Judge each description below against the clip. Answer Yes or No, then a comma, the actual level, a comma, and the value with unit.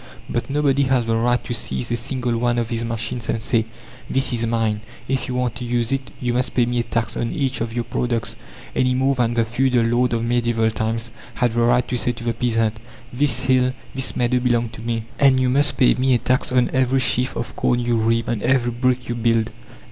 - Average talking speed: No, fast, 235 wpm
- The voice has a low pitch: Yes, low, 120 Hz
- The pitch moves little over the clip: Yes, narrow, 1.6 semitones